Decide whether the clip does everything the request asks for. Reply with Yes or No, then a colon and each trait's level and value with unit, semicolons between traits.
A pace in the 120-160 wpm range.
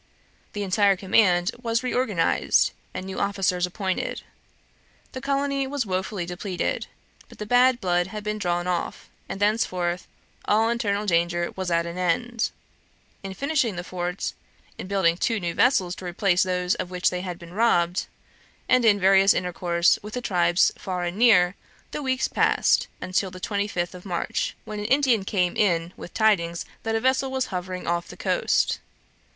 No: average, 170 wpm